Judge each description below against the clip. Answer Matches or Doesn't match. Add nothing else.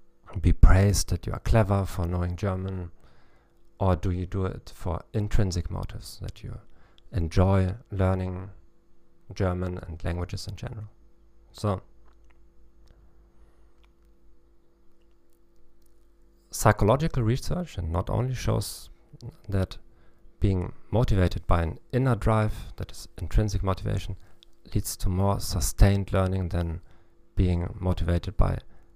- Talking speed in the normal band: Doesn't match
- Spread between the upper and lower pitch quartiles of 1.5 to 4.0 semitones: Doesn't match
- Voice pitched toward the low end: Matches